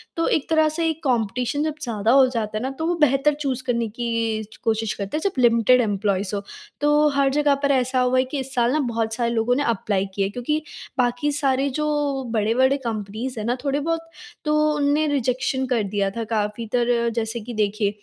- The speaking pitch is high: Yes, high, 245 Hz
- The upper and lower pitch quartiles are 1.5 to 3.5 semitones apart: No, average, 4.2 semitones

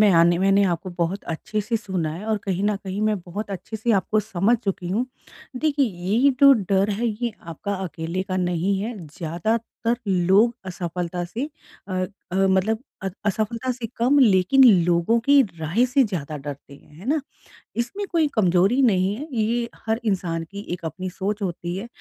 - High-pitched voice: Yes, high, 200 Hz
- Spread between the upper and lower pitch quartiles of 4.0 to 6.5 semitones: Yes, average, 4.4 semitones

